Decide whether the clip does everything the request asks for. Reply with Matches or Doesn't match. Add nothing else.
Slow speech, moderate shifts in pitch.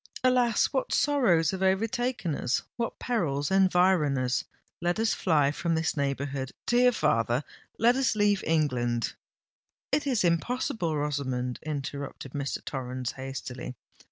Doesn't match